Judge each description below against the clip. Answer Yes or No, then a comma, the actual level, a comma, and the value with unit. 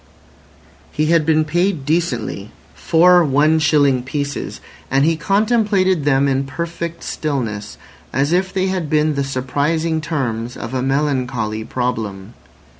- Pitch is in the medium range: Yes, medium, 145 Hz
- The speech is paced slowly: Yes, slow, 120 wpm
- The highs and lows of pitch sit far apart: No, average, 4.3 semitones